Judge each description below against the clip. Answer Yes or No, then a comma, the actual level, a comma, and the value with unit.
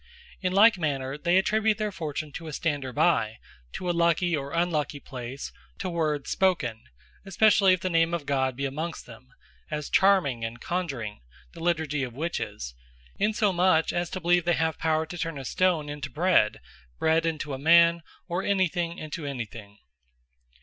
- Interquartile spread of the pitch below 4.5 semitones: Yes, average, 4.0 semitones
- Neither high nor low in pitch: Yes, medium, 160 Hz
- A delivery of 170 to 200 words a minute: Yes, average, 175 wpm